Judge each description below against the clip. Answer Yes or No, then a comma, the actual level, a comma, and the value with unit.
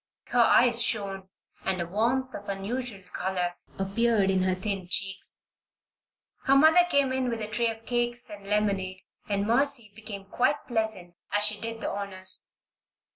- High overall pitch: Yes, high, 210 Hz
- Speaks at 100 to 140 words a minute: No, average, 160 wpm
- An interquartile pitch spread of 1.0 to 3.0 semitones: No, average, 3.8 semitones